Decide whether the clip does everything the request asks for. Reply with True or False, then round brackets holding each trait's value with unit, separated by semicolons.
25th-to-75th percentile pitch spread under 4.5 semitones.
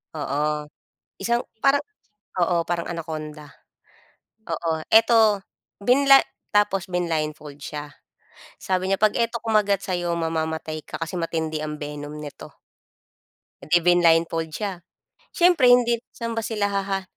False (5.1 semitones)